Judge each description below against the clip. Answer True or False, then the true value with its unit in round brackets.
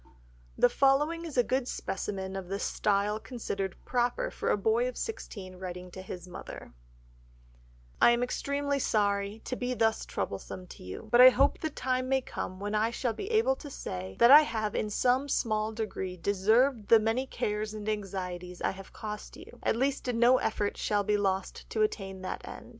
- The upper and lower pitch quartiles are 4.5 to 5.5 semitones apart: True (4.8 semitones)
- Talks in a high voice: True (215 Hz)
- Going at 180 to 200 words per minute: True (190 wpm)